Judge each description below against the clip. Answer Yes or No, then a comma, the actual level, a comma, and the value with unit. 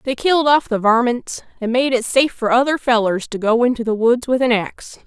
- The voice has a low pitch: No, high, 245 Hz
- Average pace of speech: No, fast, 235 wpm